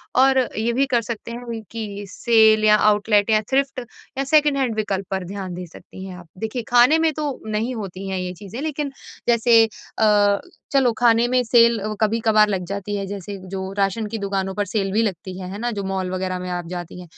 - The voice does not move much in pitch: No, average, 3.5 semitones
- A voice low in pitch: No, high, 215 Hz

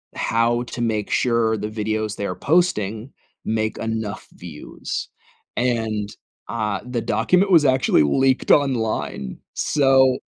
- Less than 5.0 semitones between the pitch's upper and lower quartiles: Yes, average, 3.2 semitones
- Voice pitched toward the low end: Yes, low, 115 Hz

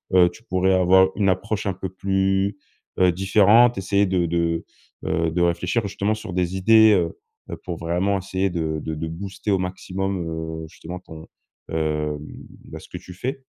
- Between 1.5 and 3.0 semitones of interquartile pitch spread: Yes, average, 2.7 semitones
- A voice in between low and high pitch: No, very low, 95 Hz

